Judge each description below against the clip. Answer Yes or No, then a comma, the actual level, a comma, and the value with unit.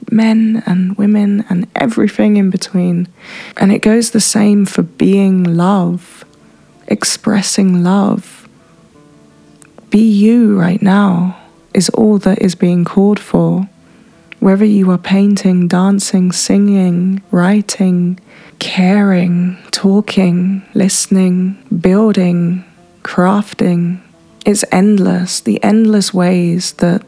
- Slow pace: Yes, slow, 100 wpm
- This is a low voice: No, high, 195 Hz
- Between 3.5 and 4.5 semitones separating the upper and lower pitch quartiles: No, narrow, 2.5 semitones